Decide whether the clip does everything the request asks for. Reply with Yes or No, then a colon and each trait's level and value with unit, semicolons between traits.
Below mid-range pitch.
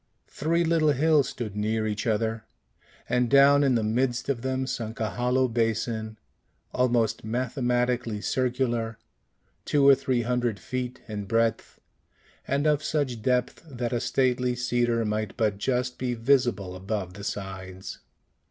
Yes: low, 120 Hz